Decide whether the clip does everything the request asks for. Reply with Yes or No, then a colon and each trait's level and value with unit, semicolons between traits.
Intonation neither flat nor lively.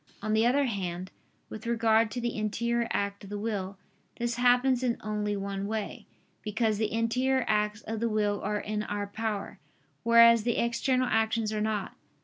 No: narrow, 2.1 semitones